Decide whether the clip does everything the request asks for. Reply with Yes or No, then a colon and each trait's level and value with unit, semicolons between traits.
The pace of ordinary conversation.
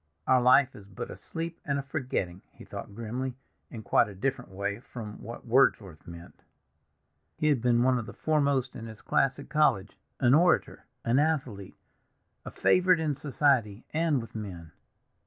Yes: average, 175 wpm